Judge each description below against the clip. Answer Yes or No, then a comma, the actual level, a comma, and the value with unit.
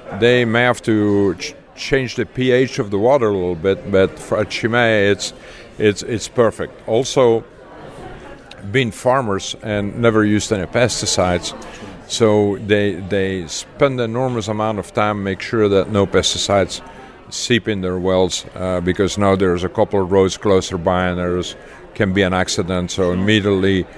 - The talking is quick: No, average, 165 wpm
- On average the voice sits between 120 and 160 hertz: No, low, 100 Hz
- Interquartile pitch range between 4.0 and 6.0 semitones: No, average, 3.1 semitones